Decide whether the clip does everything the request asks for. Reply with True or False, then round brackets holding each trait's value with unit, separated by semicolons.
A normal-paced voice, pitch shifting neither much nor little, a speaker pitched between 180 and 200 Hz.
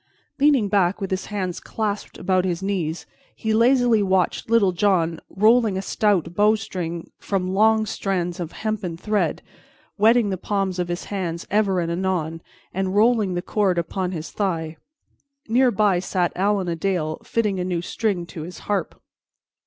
True (160 wpm; 3.1 semitones; 190 Hz)